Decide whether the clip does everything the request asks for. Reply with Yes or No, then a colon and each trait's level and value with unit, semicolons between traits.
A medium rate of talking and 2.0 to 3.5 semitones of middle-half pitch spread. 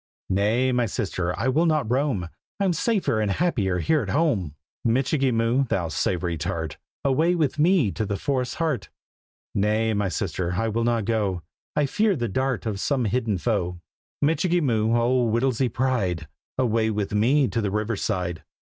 No: average, 170 wpm; average, 5.1 semitones